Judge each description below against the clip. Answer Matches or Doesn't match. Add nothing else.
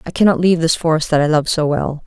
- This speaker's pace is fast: Matches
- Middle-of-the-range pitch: Matches